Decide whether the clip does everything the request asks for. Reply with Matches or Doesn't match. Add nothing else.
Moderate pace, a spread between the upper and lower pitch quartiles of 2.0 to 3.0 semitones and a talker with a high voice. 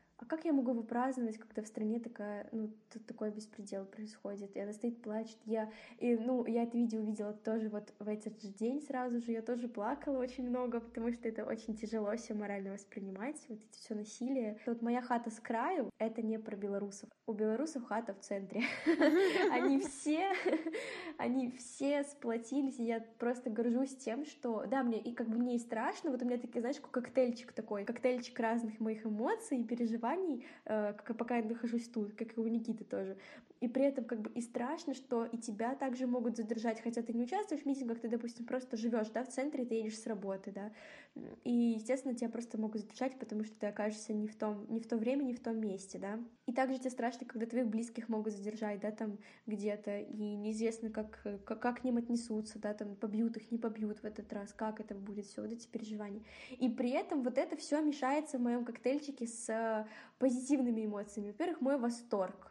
Doesn't match